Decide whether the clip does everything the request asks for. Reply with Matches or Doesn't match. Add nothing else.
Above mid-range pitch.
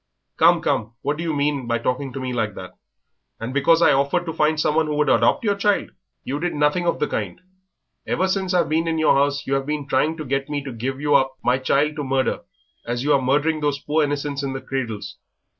Doesn't match